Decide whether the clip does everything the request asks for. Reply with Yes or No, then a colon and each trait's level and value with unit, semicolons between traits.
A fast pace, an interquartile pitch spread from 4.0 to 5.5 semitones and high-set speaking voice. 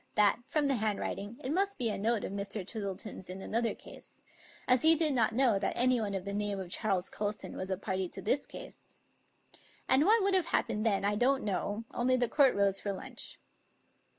Yes: fast, 210 wpm; average, 4.4 semitones; high, 215 Hz